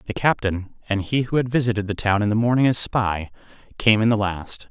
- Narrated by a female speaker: No, male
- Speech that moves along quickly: Yes, fast, 230 wpm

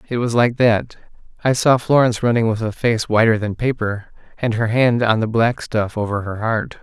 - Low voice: Yes, low, 115 Hz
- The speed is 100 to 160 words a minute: No, average, 200 wpm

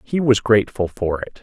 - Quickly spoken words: Yes, fast, 210 wpm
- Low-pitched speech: Yes, low, 110 Hz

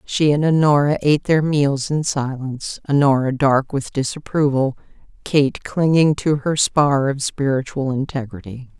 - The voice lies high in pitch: No, medium, 140 Hz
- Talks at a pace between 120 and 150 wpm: Yes, slow, 135 wpm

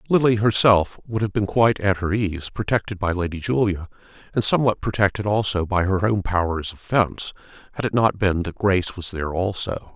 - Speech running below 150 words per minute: No, average, 195 wpm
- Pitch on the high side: No, low, 100 Hz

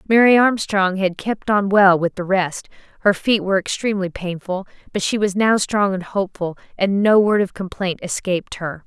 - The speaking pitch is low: No, high, 195 Hz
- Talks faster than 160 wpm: Yes, average, 190 wpm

